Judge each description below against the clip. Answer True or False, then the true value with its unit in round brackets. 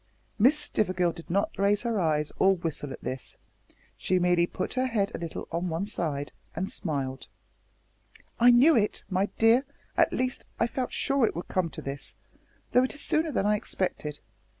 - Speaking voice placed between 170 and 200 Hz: True (190 Hz)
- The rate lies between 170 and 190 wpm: True (185 wpm)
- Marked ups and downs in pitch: True (6.0 semitones)